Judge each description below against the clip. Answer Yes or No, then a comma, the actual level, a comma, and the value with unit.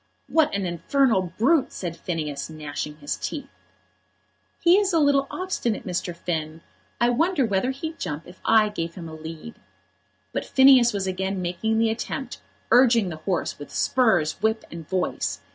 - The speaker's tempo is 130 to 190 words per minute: Yes, average, 160 wpm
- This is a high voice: Yes, high, 200 Hz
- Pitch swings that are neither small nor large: No, wide, 7.4 semitones